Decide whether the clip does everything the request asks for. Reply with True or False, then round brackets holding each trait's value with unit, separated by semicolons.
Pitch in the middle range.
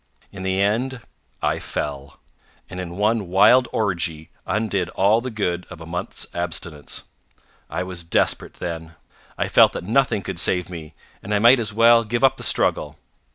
False (95 Hz)